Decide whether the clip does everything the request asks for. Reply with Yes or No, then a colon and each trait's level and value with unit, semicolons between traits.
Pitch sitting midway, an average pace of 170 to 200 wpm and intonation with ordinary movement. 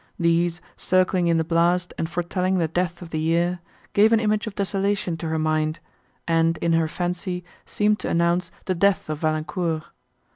No: medium, 175 Hz; average, 180 wpm; narrow, 2.1 semitones